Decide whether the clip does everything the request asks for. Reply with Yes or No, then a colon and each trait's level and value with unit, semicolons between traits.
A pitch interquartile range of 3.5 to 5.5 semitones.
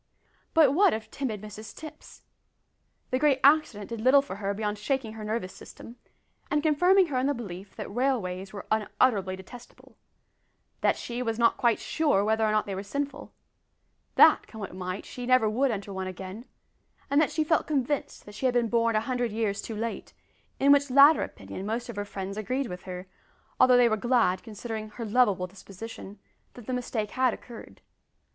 Yes: average, 4.1 semitones